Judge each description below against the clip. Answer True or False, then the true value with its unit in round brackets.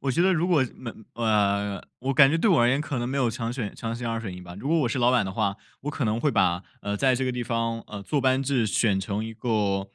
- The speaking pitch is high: False (115 Hz)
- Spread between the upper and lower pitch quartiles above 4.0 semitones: True (4.4 semitones)